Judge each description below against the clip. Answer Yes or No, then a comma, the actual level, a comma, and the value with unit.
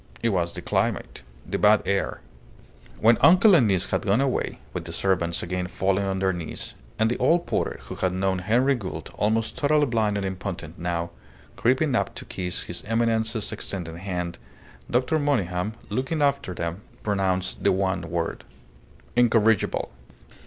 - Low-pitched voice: Yes, low, 100 Hz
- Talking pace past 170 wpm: No, average, 160 wpm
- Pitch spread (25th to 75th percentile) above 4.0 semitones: Yes, average, 4.6 semitones